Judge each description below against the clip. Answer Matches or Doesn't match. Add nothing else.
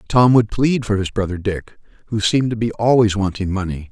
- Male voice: Matches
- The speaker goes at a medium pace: Doesn't match